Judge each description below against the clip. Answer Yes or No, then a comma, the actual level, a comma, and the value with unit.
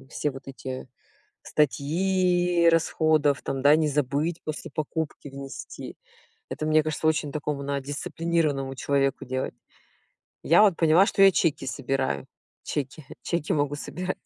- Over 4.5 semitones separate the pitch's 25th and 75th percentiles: No, average, 3.1 semitones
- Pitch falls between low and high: Yes, medium, 150 Hz